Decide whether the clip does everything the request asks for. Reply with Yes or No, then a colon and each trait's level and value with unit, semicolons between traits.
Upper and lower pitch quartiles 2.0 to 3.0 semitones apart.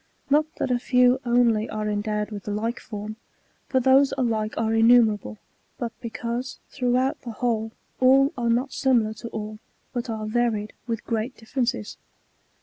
Yes: narrow, 2.6 semitones